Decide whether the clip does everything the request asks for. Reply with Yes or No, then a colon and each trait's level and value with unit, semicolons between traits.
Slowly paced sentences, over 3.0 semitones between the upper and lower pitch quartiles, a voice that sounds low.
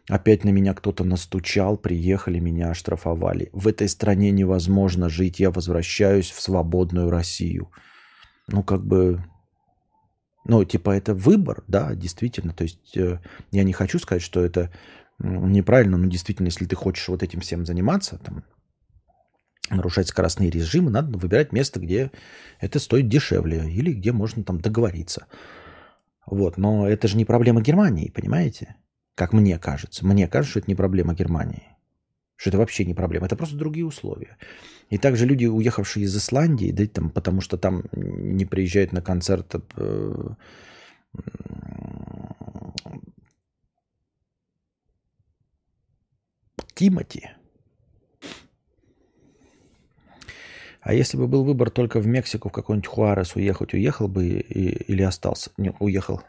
No: average, 130 wpm; average, 3.5 semitones; very low, 95 Hz